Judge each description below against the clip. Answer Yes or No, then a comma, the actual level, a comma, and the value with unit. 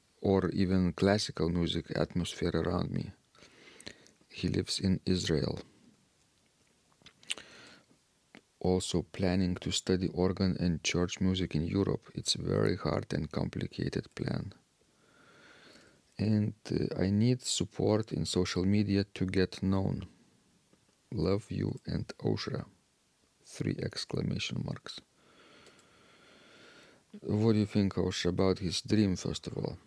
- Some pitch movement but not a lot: No, narrow, 2.0 semitones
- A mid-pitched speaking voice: No, very low, 95 Hz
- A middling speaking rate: No, slow, 115 wpm